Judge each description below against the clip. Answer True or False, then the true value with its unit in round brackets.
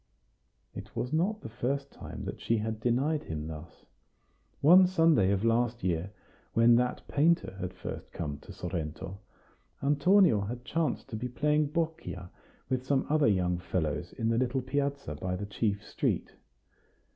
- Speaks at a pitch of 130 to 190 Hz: False (120 Hz)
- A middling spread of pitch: False (7.4 semitones)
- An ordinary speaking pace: True (155 wpm)